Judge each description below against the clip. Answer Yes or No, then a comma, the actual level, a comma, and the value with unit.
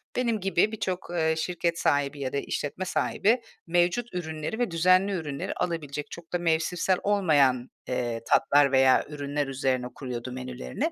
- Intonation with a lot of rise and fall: No, average, 4.8 semitones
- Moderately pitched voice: Yes, medium, 160 Hz